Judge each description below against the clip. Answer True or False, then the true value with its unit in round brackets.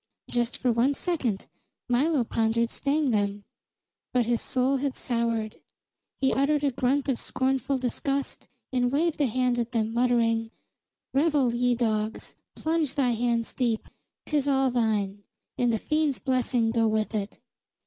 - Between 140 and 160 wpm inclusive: True (150 wpm)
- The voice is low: False (245 Hz)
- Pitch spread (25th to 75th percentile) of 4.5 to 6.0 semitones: False (3.2 semitones)